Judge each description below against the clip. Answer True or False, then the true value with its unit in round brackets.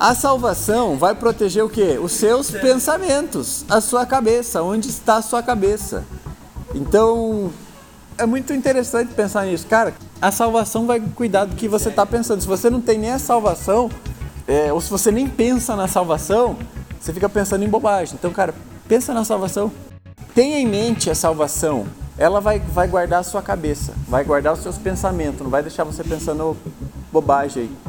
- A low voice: False (205 Hz)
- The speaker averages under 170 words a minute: False (175 wpm)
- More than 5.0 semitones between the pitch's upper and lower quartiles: True (5.4 semitones)